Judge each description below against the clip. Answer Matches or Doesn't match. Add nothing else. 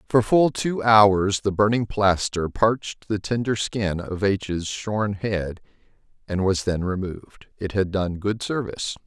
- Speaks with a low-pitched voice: Matches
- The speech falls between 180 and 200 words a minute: Doesn't match